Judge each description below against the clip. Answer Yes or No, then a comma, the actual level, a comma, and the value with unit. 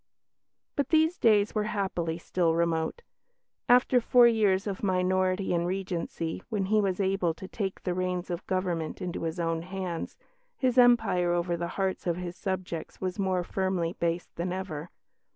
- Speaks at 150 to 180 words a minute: Yes, average, 165 wpm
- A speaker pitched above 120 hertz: Yes, medium, 185 Hz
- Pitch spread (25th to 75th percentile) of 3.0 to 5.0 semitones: No, narrow, 2.5 semitones